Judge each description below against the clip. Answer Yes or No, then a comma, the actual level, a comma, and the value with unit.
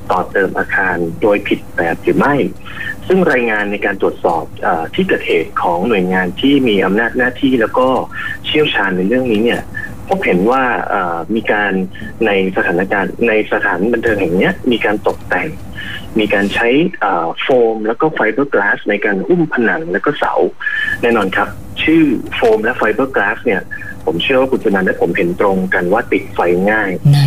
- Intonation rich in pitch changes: Yes, wide, 9.0 semitones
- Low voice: Yes, low, 130 Hz